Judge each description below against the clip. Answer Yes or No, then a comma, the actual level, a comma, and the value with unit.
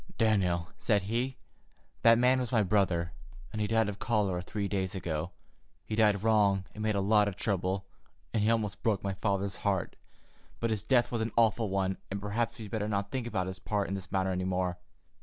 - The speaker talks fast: Yes, fast, 210 wpm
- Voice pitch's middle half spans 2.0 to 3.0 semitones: Yes, average, 2.7 semitones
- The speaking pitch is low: Yes, low, 100 Hz